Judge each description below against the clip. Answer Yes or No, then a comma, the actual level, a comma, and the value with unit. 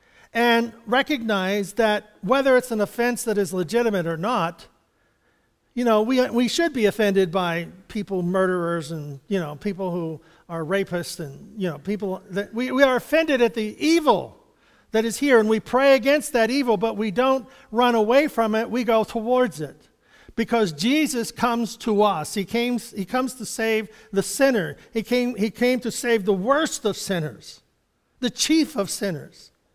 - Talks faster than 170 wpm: Yes, average, 180 wpm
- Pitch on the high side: Yes, high, 220 Hz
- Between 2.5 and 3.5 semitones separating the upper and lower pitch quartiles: No, average, 4.0 semitones